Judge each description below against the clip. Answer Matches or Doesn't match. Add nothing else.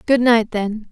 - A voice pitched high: Matches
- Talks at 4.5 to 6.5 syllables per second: Doesn't match